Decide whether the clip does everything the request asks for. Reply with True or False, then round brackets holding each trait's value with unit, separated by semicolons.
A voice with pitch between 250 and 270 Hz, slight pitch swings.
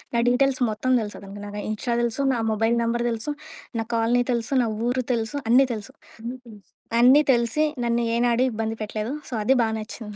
False (235 Hz; 1.9 semitones)